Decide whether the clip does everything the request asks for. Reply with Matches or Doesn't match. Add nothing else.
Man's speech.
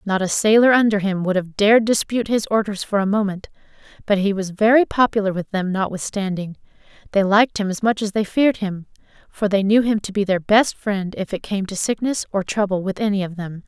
Doesn't match